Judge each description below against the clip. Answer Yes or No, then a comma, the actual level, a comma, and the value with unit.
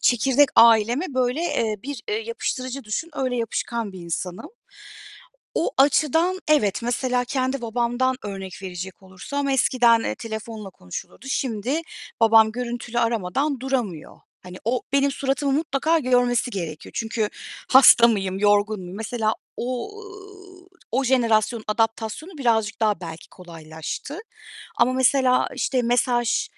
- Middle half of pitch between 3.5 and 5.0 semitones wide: Yes, average, 3.8 semitones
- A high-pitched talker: Yes, high, 240 Hz